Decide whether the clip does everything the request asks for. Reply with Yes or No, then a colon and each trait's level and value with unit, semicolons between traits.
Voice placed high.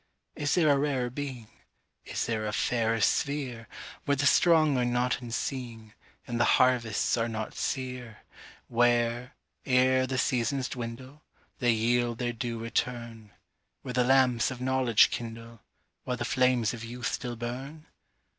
No: low, 120 Hz